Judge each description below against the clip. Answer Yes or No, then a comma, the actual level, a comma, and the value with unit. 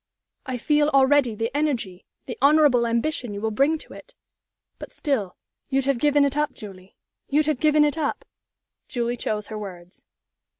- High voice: Yes, very high, 265 Hz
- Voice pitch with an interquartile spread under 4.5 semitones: No, average, 5.0 semitones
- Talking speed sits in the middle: Yes, average, 170 wpm